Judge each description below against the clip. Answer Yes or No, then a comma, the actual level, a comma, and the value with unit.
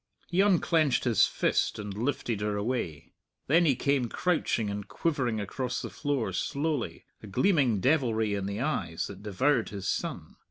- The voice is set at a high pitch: No, low, 120 Hz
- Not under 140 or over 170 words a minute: Yes, average, 160 wpm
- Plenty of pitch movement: Yes, wide, 6.0 semitones